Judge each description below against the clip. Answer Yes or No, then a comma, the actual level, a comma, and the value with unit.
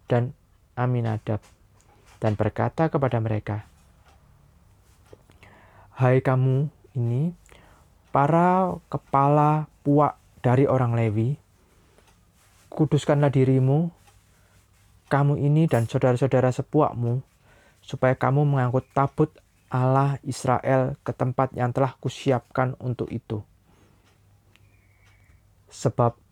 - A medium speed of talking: No, slow, 80 wpm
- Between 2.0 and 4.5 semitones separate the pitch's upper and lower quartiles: No, average, 5.1 semitones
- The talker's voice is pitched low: Yes, low, 120 Hz